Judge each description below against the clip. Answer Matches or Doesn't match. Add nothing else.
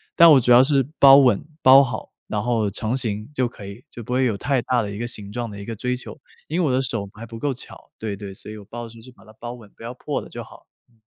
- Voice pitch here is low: Matches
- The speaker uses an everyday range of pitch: Matches